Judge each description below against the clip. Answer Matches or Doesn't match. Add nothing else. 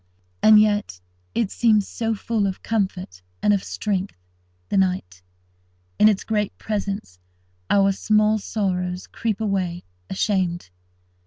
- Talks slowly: Matches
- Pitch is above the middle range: Matches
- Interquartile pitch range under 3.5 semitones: Matches